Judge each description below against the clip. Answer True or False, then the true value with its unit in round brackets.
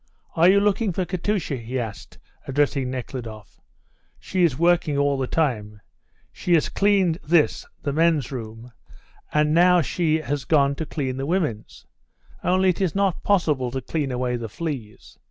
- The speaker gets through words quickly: False (160 wpm)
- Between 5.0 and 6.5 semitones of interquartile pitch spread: True (5.5 semitones)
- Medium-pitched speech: True (150 Hz)